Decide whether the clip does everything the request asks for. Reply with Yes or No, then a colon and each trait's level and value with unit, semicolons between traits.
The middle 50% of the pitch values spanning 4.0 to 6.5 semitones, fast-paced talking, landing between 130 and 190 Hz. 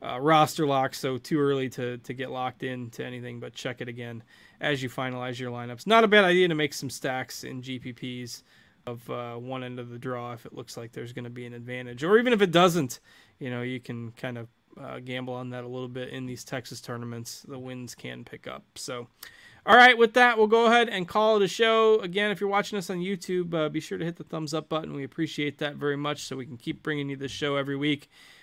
Yes: average, 4.7 semitones; fast, 255 wpm; low, 135 Hz